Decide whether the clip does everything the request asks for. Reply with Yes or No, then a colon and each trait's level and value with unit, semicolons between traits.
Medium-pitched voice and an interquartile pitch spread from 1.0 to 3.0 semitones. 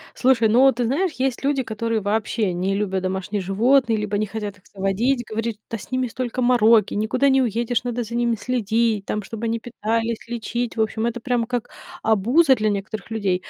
No: high, 225 Hz; narrow, 2.6 semitones